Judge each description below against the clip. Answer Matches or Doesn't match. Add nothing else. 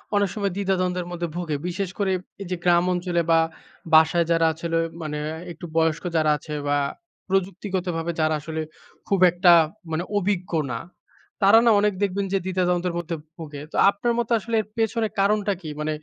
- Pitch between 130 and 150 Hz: Doesn't match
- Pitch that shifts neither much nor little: Matches